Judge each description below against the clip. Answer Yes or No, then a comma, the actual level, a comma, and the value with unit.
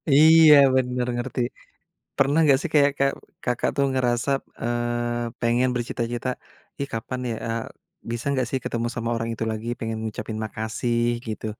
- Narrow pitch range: Yes, narrow, 2.2 semitones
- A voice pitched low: Yes, low, 120 Hz